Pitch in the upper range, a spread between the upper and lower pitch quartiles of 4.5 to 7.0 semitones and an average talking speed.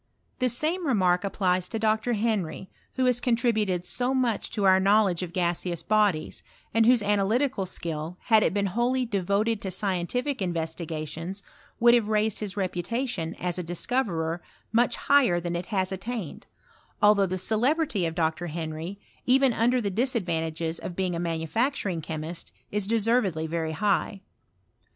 Yes: high, 195 Hz; average, 4.9 semitones; average, 150 wpm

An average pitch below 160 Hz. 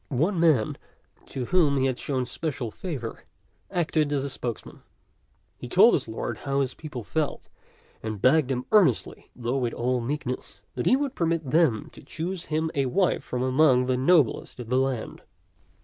Yes: low, 135 Hz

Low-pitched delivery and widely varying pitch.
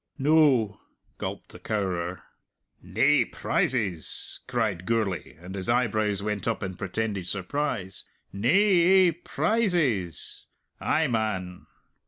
Yes: low, 110 Hz; wide, 7.0 semitones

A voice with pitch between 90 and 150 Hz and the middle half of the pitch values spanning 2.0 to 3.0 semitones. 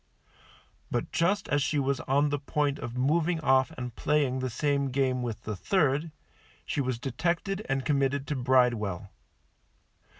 Yes: low, 135 Hz; average, 2.7 semitones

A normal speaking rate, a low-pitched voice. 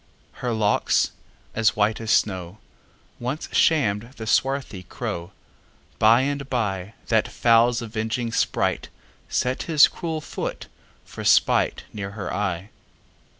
No: slow, 100 wpm; low, 110 Hz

